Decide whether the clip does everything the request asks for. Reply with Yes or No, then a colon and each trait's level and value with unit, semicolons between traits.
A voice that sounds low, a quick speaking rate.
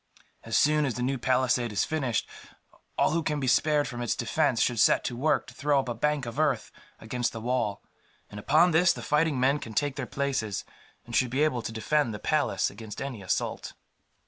Yes: low, 130 Hz; fast, 215 wpm